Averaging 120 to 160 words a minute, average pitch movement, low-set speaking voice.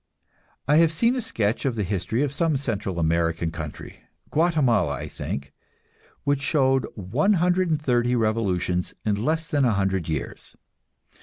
No: average, 140 wpm; wide, 8.5 semitones; low, 120 Hz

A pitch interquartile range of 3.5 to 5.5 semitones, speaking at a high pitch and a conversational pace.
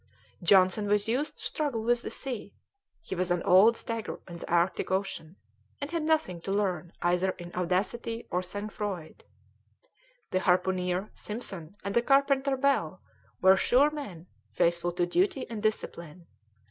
Yes: average, 5.1 semitones; high, 195 Hz; average, 155 wpm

